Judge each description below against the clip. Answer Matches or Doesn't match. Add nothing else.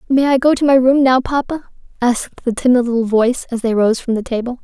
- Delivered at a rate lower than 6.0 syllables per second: Doesn't match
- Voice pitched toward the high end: Matches